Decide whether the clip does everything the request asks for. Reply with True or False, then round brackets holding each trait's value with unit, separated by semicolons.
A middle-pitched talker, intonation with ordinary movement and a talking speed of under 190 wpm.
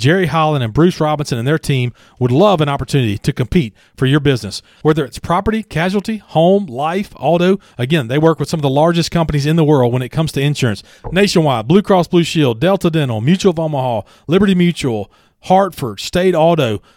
False (155 Hz; 4.8 semitones; 200 wpm)